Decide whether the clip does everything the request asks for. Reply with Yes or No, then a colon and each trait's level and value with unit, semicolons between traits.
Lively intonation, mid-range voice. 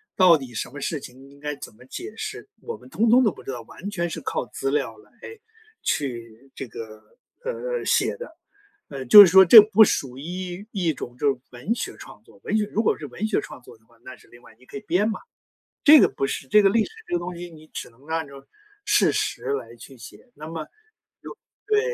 Yes: wide, 8.2 semitones; medium, 155 Hz